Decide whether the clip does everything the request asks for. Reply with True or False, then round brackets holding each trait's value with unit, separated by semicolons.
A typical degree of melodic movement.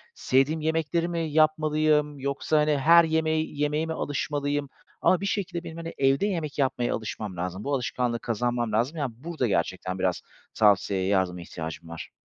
False (6.1 semitones)